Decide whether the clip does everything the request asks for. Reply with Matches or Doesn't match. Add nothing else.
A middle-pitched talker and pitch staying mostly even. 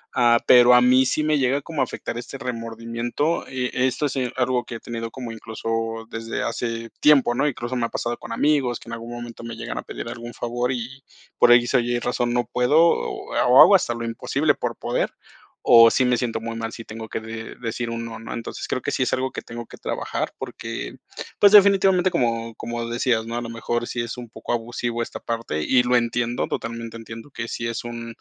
Doesn't match